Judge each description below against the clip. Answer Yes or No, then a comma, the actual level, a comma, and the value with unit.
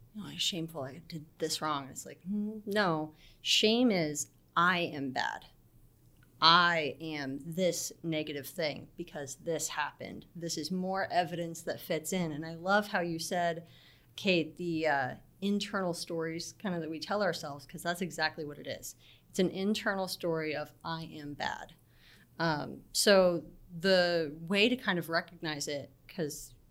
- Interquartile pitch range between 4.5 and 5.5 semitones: No, average, 3.1 semitones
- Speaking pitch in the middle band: Yes, medium, 165 Hz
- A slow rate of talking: No, average, 160 wpm